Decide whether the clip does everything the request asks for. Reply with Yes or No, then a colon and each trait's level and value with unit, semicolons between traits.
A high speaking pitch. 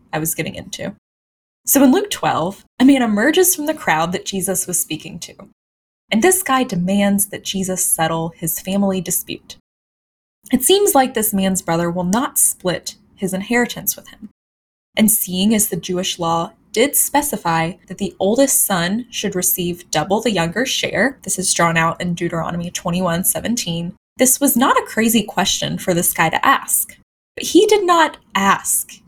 Yes: high, 195 Hz